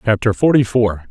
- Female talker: No, male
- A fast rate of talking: No, average, 165 wpm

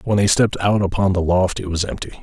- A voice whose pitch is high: No, very low, 95 Hz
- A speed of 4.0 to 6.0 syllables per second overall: No, 6.4 syllables/s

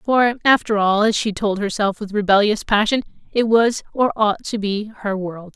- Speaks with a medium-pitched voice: No, high, 210 Hz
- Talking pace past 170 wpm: Yes, average, 195 wpm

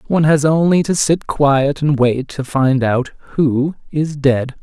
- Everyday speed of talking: Yes, average, 180 wpm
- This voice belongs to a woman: No, male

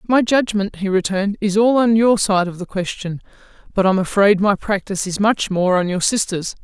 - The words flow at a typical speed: No, fast, 215 wpm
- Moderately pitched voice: No, high, 200 Hz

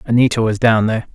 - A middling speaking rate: No, fast, 210 wpm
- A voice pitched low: Yes, low, 115 Hz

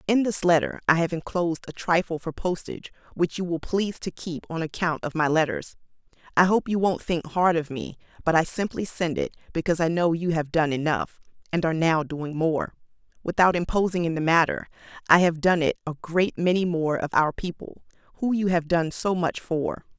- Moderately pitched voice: Yes, medium, 170 Hz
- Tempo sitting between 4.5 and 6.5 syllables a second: Yes, 5.4 syllables/s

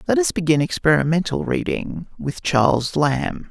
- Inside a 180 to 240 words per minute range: No, slow, 135 wpm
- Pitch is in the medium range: Yes, medium, 155 Hz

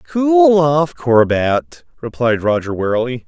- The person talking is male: Yes, male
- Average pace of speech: No, slow, 110 wpm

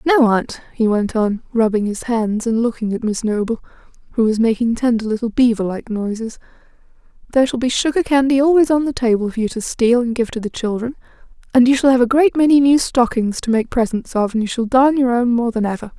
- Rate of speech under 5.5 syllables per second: No, 5.8 syllables/s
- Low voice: No, high, 240 Hz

